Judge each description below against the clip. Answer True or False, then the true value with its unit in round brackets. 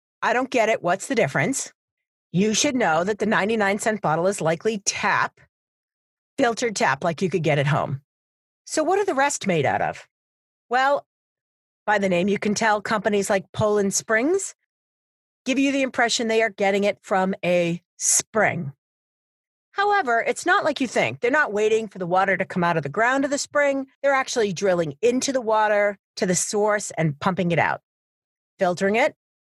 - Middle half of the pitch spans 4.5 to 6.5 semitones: True (5.2 semitones)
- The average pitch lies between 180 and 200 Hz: False (215 Hz)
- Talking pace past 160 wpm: True (185 wpm)